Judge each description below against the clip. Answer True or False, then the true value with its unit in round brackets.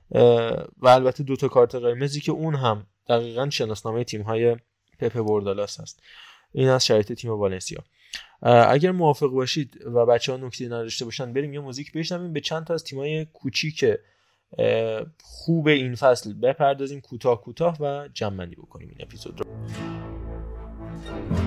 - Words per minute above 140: True (150 wpm)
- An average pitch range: True (4.2 semitones)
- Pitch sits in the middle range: False (125 Hz)